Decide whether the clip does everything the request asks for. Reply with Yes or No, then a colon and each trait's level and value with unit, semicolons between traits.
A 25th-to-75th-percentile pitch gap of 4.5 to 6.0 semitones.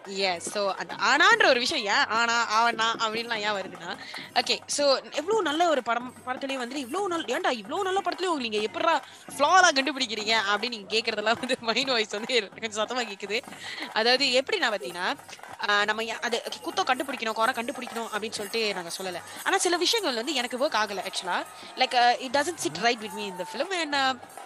Yes: average, 4.8 semitones